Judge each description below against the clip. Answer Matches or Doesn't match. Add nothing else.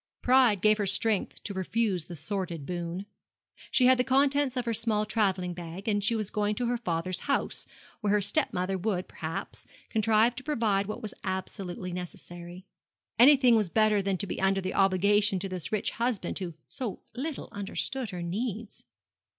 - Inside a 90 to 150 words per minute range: Doesn't match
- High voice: Matches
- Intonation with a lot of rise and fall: Doesn't match